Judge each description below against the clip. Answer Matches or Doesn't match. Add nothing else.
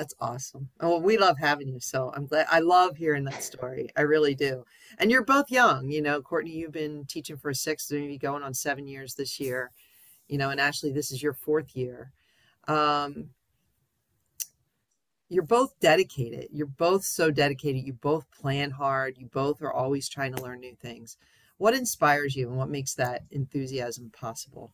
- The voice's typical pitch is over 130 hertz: Matches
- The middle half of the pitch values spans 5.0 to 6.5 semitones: Doesn't match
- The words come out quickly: Doesn't match